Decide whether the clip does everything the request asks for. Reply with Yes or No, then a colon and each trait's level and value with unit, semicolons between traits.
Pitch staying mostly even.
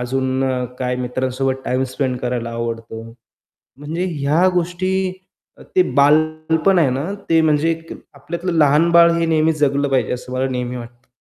No: average, 4.3 semitones